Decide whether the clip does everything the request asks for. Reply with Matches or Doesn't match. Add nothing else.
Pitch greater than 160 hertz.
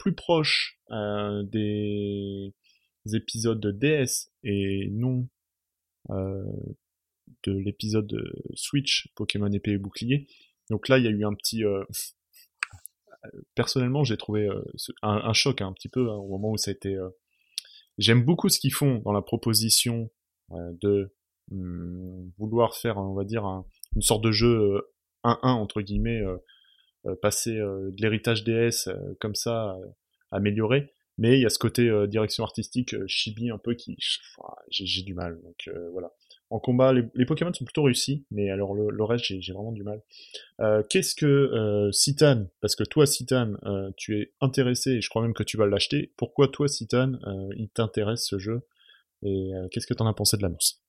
Doesn't match